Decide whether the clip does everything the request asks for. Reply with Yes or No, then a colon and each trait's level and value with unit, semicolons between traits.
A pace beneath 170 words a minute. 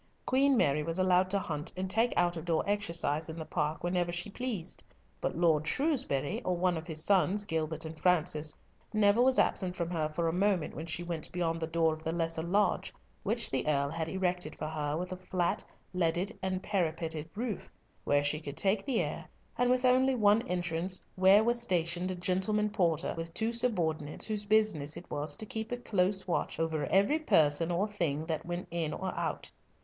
No: average, 200 wpm